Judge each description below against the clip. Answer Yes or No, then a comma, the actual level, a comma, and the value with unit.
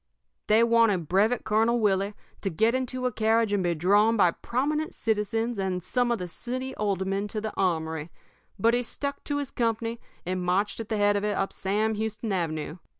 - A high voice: Yes, high, 215 Hz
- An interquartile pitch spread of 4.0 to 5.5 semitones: No, average, 3.3 semitones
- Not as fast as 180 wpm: No, average, 195 wpm